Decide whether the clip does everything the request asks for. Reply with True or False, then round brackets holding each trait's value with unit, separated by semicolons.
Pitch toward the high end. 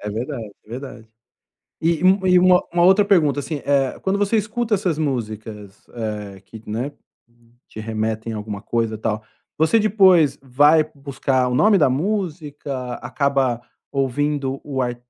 False (140 Hz)